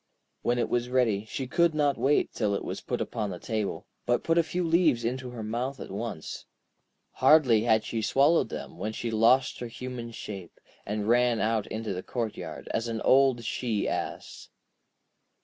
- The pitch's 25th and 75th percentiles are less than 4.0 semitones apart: Yes, average, 3.1 semitones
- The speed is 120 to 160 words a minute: No, average, 185 wpm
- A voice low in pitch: Yes, low, 120 Hz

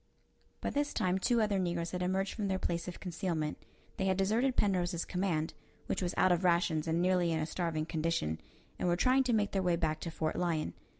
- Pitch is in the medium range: Yes, medium, 180 Hz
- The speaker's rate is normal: No, fast, 220 wpm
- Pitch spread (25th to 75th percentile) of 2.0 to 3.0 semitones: Yes, narrow, 2.5 semitones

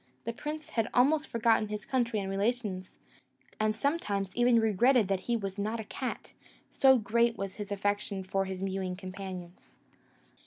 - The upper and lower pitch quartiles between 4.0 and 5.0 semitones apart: No, average, 3.5 semitones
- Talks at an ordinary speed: Yes, average, 160 wpm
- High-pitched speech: Yes, high, 210 Hz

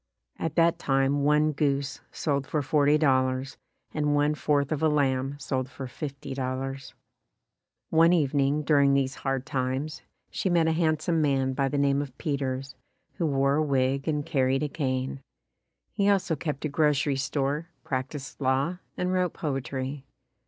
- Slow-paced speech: No, average, 160 wpm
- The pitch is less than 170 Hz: Yes, medium, 140 Hz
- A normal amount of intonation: No, narrow, 2.2 semitones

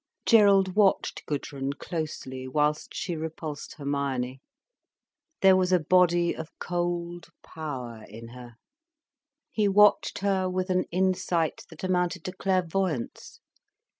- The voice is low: No, medium, 170 Hz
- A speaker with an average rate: No, slow, 115 wpm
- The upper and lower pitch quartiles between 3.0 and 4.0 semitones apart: No, average, 4.5 semitones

